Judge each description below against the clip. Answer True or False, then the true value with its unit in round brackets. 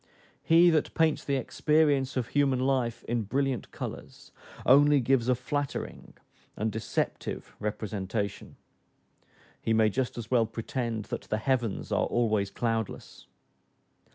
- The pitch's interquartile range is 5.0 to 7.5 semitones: False (3.6 semitones)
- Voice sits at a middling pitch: False (120 Hz)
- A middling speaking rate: False (125 wpm)